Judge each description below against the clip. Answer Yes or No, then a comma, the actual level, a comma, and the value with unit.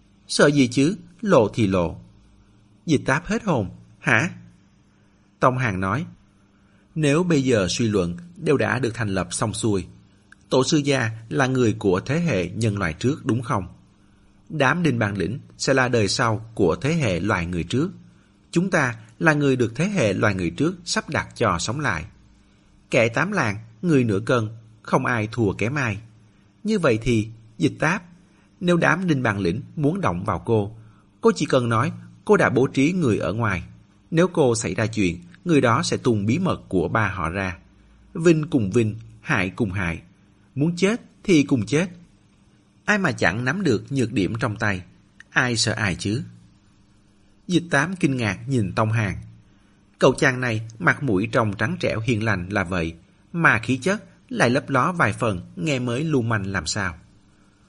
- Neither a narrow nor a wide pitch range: No, wide, 6.1 semitones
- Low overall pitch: Yes, low, 115 Hz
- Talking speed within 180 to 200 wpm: Yes, average, 185 wpm